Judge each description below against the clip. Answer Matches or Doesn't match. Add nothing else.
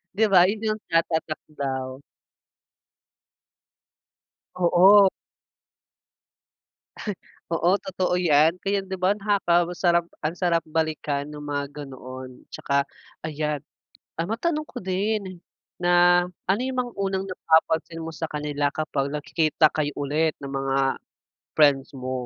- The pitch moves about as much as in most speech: Matches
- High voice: Doesn't match